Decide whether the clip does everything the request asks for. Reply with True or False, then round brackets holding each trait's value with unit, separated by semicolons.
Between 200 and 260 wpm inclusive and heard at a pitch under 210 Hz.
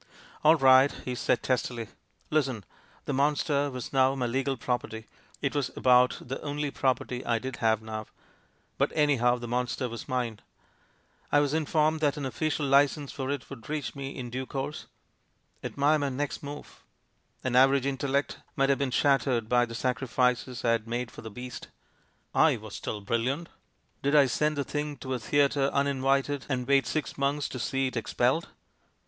False (190 wpm; 135 Hz)